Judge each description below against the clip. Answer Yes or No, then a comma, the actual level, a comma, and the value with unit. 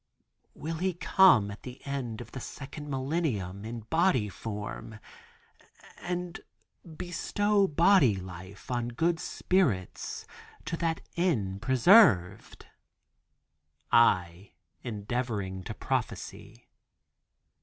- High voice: No, low, 125 Hz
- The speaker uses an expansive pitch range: Yes, wide, 8.6 semitones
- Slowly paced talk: Yes, slow, 95 wpm